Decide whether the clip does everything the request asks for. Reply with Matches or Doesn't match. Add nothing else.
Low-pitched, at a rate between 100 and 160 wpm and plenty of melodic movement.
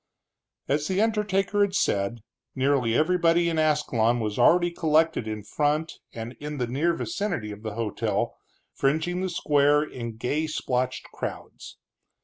Doesn't match